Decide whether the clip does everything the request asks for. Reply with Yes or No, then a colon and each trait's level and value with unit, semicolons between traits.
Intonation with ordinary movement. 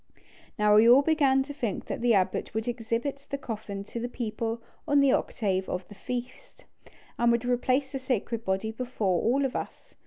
Yes: average, 3.5 semitones